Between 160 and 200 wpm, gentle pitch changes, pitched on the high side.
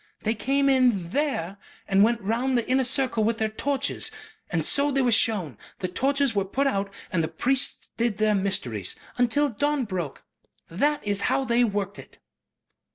No: average, 175 wpm; average, 5.2 semitones; high, 230 Hz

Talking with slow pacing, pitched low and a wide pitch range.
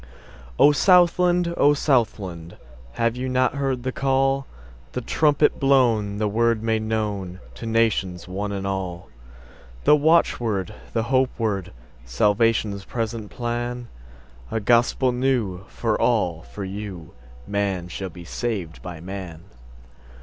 Yes: slow, 105 wpm; low, 105 Hz; wide, 5.7 semitones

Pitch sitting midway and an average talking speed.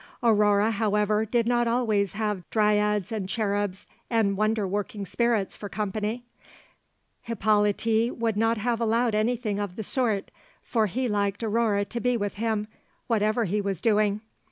No: high, 215 Hz; average, 150 wpm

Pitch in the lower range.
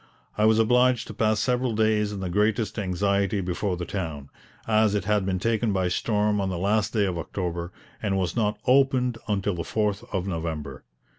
Yes: low, 105 Hz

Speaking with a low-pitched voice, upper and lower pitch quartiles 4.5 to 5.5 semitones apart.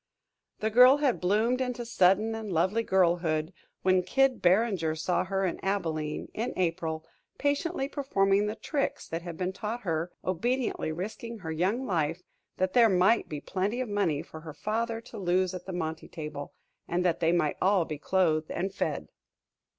No: medium, 185 Hz; average, 5.2 semitones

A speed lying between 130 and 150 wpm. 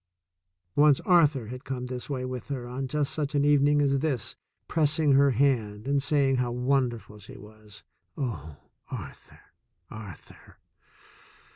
Yes: average, 140 wpm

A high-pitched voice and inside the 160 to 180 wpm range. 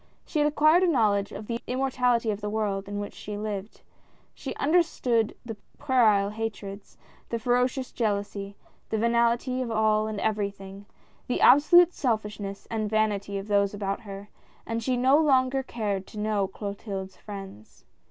Yes: high, 215 Hz; average, 170 wpm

